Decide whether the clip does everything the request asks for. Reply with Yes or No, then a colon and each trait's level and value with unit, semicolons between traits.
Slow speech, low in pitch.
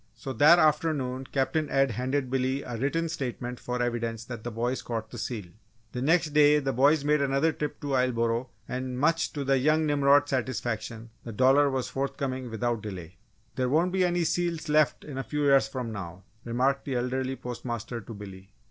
No: average, 185 wpm; low, 130 Hz